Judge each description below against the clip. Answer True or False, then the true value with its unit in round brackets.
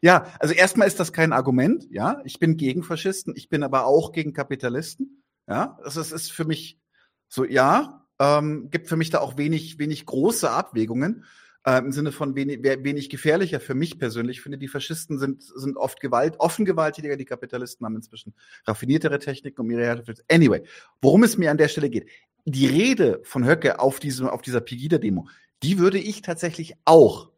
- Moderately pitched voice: True (145 Hz)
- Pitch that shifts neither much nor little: True (3.6 semitones)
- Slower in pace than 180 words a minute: False (190 wpm)